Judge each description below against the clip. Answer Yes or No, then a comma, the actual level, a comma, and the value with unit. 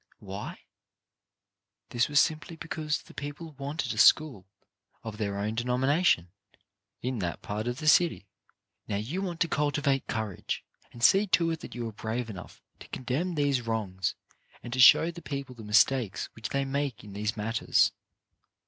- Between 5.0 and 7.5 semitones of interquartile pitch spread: Yes, wide, 5.6 semitones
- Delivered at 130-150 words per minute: No, average, 160 wpm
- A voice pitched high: No, low, 125 Hz